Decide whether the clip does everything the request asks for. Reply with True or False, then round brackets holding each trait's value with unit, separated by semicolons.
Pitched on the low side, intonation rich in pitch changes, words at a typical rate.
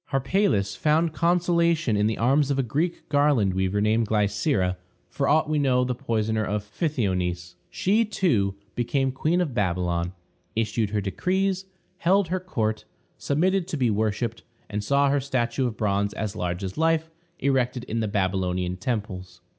True (120 Hz; 7.0 semitones; 160 wpm)